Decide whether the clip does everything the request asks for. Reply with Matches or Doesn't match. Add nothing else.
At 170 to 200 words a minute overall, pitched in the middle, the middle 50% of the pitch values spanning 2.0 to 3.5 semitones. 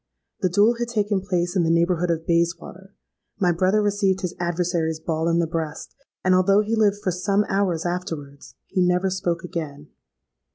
Matches